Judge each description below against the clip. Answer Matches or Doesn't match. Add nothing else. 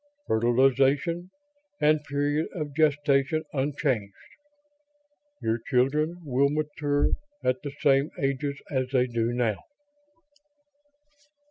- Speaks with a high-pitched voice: Doesn't match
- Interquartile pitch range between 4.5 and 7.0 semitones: Doesn't match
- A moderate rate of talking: Doesn't match